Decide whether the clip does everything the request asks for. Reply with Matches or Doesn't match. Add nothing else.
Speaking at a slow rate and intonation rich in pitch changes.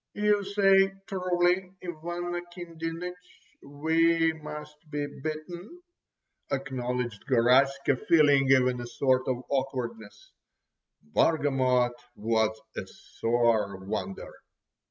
Matches